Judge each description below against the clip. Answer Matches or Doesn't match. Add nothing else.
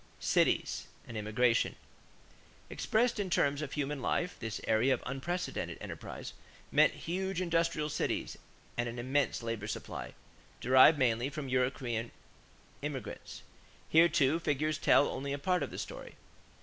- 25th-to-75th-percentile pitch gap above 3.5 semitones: Matches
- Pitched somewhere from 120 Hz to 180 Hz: Matches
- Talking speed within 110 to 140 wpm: Matches